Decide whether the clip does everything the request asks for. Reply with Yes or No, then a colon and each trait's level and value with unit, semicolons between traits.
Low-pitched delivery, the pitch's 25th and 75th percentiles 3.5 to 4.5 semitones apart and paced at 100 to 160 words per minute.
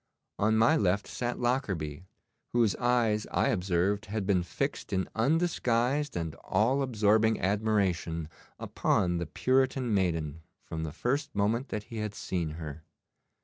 No: low, 105 Hz; average, 5.2 semitones; average, 140 wpm